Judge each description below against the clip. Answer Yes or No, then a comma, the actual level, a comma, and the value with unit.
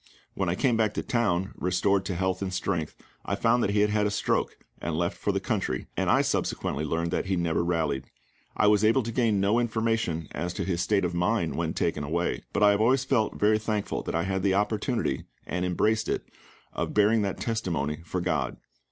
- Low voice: Yes, low, 100 Hz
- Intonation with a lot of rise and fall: No, average, 3.9 semitones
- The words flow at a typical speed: No, fast, 220 wpm